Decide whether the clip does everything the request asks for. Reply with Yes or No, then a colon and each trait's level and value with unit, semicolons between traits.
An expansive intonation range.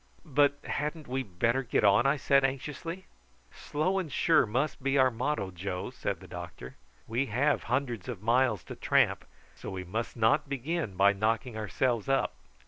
No: average, 4.7 semitones